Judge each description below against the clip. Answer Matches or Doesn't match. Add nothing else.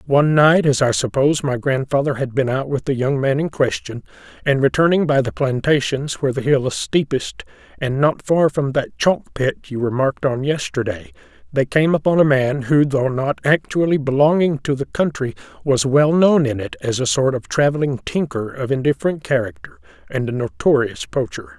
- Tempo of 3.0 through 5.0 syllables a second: Doesn't match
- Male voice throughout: Matches